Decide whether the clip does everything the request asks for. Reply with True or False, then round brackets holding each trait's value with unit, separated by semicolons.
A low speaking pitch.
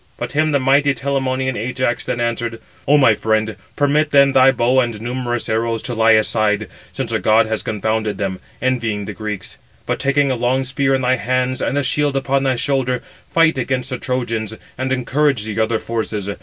True (125 Hz)